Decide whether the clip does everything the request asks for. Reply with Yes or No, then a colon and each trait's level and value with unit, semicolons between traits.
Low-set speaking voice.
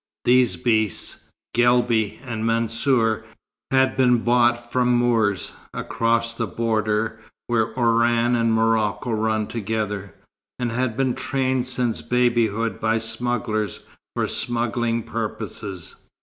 Yes: low, 115 Hz